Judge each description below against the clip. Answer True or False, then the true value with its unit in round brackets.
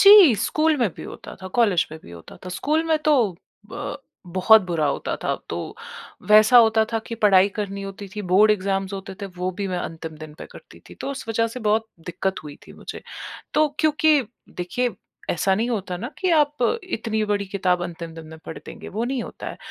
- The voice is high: True (210 Hz)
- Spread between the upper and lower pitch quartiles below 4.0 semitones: False (5.1 semitones)